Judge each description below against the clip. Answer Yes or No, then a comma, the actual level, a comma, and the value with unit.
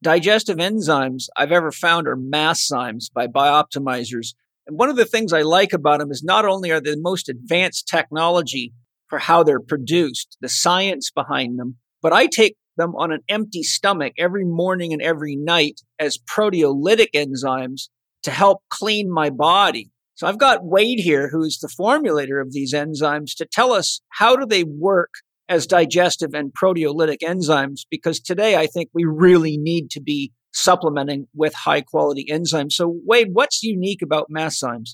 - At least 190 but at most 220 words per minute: No, average, 175 wpm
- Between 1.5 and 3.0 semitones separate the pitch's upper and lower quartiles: No, average, 3.8 semitones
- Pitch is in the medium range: Yes, medium, 160 Hz